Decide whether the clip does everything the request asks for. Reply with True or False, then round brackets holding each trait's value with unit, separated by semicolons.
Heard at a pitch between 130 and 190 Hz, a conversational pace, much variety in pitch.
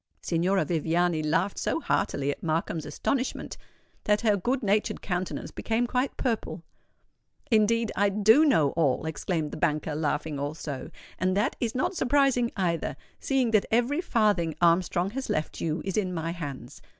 True (185 Hz; 155 wpm; 6.2 semitones)